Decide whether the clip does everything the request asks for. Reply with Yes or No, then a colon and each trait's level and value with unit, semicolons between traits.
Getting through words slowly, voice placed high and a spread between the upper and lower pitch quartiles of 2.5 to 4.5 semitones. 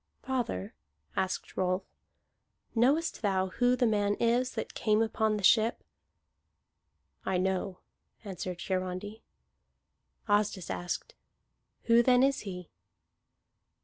Yes: slow, 105 wpm; high, 205 Hz; average, 4.0 semitones